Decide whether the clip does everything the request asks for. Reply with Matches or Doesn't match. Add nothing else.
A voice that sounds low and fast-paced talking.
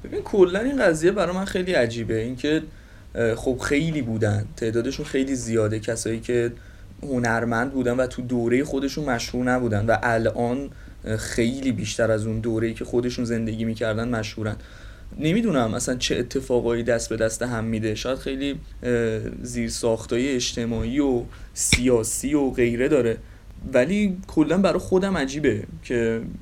Doesn't match